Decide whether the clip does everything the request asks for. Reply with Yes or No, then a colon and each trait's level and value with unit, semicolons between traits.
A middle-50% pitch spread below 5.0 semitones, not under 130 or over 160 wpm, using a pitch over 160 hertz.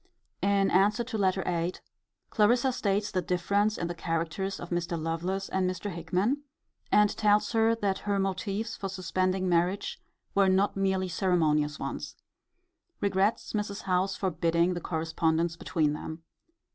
Yes: average, 2.9 semitones; average, 145 wpm; high, 190 Hz